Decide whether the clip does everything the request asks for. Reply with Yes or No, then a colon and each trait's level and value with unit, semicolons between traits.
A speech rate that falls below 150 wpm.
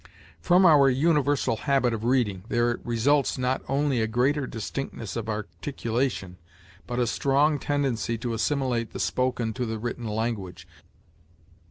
Yes: average, 140 wpm